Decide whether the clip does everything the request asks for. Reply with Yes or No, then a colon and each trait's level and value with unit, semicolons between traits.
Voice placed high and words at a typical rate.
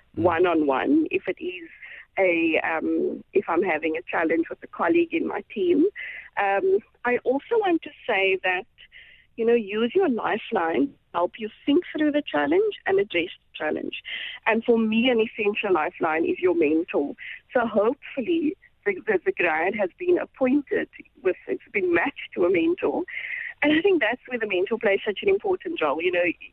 Yes: very high, 275 Hz; average, 185 wpm